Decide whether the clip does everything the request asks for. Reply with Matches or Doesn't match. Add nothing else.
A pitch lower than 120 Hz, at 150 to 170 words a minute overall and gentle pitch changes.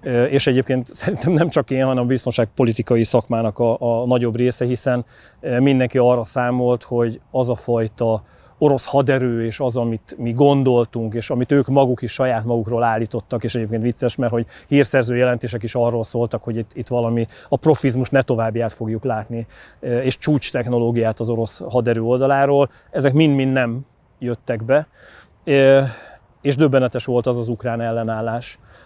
Doesn't match